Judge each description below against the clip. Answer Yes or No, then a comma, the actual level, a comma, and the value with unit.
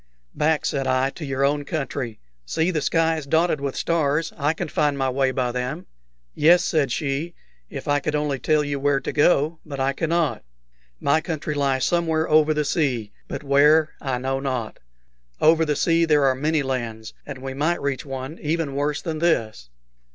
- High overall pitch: No, medium, 145 Hz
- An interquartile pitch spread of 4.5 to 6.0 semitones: No, average, 2.8 semitones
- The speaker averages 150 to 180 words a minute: No, average, 190 wpm